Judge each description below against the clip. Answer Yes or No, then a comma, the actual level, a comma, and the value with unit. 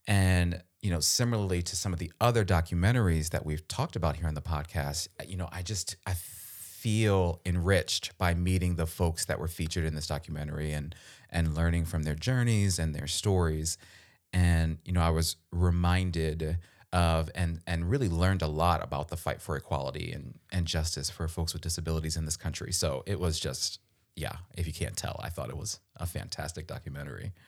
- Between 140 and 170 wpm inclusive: No, average, 190 wpm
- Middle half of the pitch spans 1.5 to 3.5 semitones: Yes, average, 2.8 semitones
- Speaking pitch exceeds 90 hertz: No, very low, 85 Hz